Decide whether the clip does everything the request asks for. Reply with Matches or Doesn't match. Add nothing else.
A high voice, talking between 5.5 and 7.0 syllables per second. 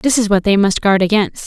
Matches